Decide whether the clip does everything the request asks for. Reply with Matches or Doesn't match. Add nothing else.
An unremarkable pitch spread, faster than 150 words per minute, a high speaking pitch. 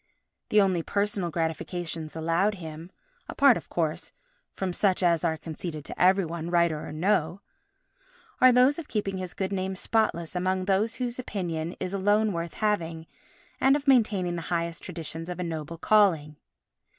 Doesn't match